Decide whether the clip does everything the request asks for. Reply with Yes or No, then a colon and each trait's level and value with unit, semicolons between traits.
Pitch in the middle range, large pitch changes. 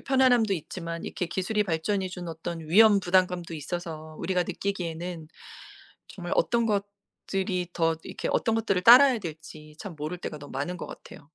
No: medium, 180 Hz; average, 3.6 semitones